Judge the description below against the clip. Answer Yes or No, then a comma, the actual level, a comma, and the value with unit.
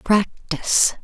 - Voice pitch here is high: Yes, high, 195 Hz